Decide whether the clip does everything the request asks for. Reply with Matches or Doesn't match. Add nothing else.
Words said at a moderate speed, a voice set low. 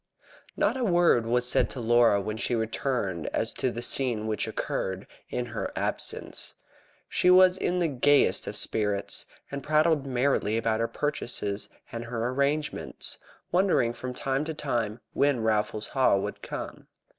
Matches